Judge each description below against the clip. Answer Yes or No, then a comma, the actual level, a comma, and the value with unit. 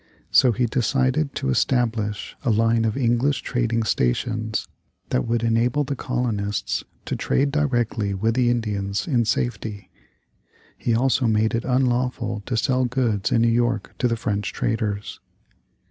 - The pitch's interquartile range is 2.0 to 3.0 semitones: Yes, narrow, 2.5 semitones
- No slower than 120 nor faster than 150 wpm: Yes, average, 145 wpm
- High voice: No, low, 115 Hz